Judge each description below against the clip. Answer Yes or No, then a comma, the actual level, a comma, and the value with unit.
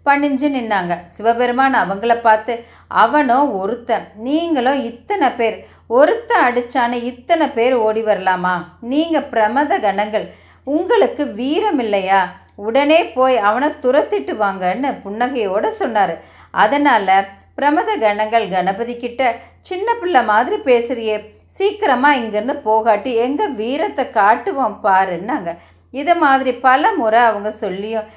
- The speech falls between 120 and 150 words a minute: No, average, 110 wpm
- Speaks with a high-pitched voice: Yes, high, 245 Hz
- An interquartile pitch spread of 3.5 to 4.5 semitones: No, average, 5.2 semitones